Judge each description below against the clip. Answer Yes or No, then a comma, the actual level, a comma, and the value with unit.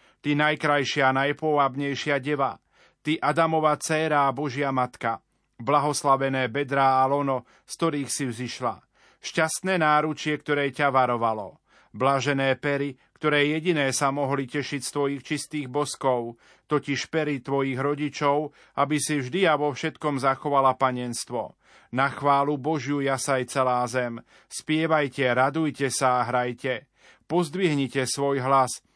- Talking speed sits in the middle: Yes, average, 125 wpm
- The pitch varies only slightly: Yes, narrow, 2.0 semitones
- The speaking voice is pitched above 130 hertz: Yes, medium, 140 Hz